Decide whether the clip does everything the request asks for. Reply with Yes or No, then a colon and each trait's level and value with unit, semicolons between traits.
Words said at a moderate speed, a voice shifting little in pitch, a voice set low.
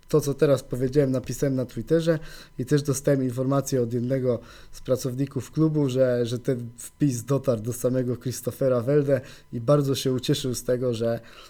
No: fast, 165 wpm; narrow, 2.3 semitones; low, 130 Hz